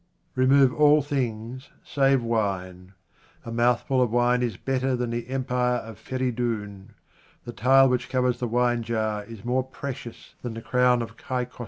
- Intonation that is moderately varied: No, narrow, 2.1 semitones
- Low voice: Yes, low, 125 Hz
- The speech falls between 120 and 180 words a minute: Yes, average, 165 wpm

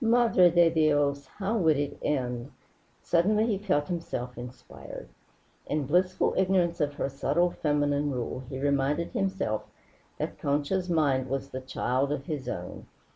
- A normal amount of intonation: Yes, average, 4.5 semitones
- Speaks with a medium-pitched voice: Yes, medium, 145 Hz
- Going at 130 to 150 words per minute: Yes, average, 145 wpm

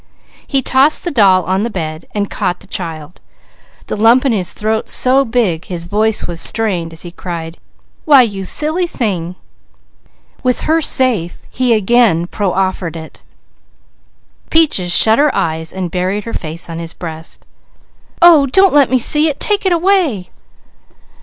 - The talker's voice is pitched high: Yes, high, 205 Hz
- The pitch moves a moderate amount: No, wide, 7.1 semitones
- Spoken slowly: No, average, 160 wpm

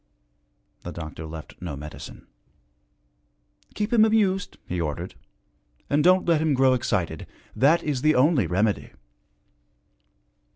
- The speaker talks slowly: Yes, slow, 120 wpm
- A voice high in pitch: No, low, 130 Hz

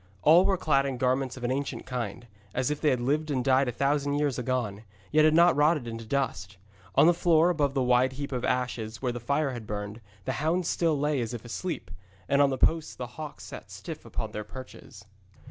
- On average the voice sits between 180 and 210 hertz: No, low, 135 Hz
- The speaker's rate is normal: No, fast, 225 wpm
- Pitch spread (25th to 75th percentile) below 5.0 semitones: Yes, average, 3.5 semitones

